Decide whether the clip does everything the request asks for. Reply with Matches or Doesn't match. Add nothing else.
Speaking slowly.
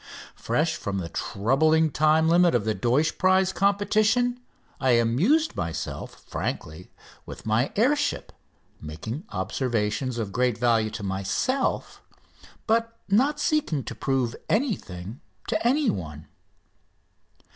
Matches